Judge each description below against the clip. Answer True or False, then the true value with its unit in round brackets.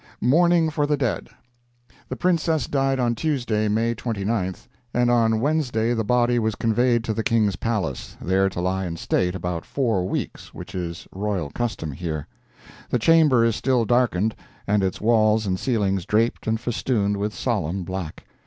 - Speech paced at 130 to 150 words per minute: False (165 wpm)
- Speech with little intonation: False (4.2 semitones)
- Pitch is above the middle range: False (110 Hz)